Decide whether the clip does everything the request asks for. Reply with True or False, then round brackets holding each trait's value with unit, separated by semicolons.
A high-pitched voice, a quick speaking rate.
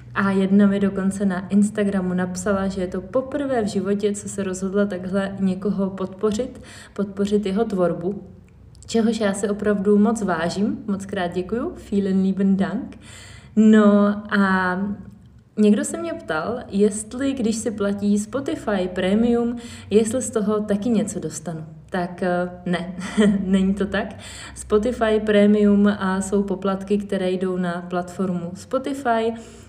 False (200 Hz; 135 wpm)